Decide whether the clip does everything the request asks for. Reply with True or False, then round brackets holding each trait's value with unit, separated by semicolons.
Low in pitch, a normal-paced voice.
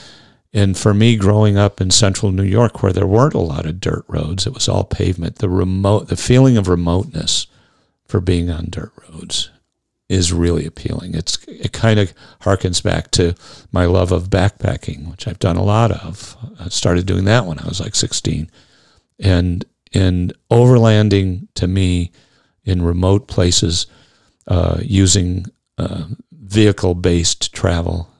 True (95 Hz; 160 wpm)